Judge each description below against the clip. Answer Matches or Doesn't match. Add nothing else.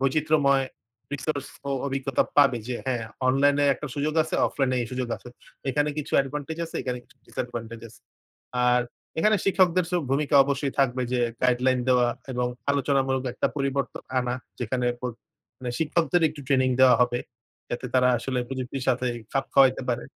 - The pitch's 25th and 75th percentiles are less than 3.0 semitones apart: Matches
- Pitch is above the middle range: Doesn't match